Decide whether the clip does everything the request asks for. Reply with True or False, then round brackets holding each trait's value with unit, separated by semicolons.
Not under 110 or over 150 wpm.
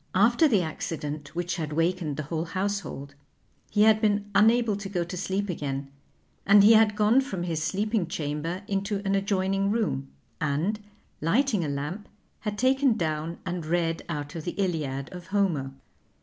False (165 wpm)